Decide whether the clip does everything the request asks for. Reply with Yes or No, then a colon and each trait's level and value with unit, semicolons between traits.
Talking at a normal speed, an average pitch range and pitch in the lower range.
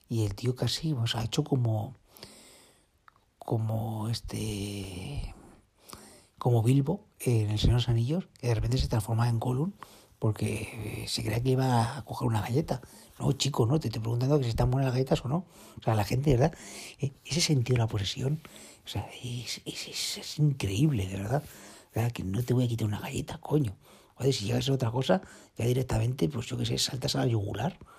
No: fast, 205 wpm; average, 3.5 semitones; low, 120 Hz